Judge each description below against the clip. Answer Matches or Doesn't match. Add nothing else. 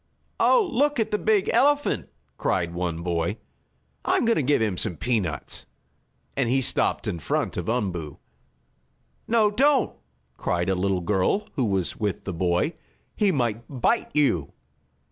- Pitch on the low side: Matches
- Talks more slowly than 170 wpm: Matches